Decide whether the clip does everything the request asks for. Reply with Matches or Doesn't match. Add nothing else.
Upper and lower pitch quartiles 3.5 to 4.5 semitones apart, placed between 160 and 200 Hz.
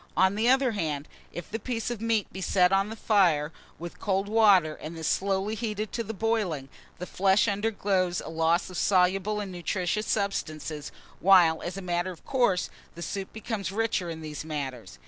Matches